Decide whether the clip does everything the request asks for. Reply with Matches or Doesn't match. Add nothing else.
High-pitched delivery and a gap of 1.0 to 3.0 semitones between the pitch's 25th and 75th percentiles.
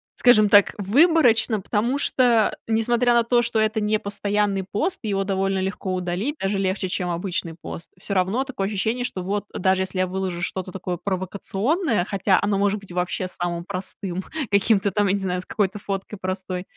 Matches